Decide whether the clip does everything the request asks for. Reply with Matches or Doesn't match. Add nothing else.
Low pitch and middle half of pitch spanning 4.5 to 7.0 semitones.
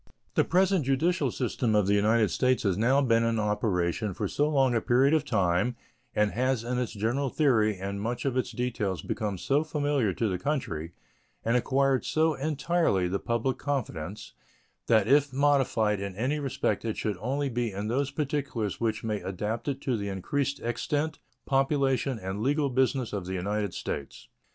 Matches